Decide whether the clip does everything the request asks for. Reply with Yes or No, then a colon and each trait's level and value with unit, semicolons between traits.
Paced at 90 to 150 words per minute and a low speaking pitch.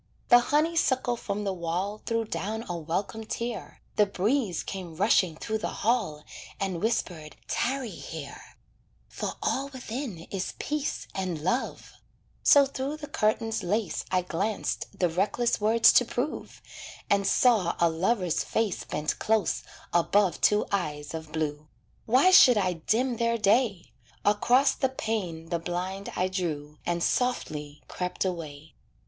No: average, 140 wpm; high, 200 Hz